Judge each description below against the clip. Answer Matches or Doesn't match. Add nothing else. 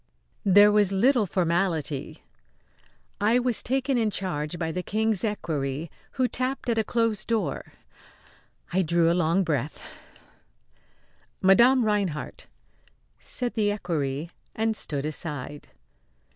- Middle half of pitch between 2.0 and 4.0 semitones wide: Doesn't match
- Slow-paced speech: Matches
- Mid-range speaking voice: Doesn't match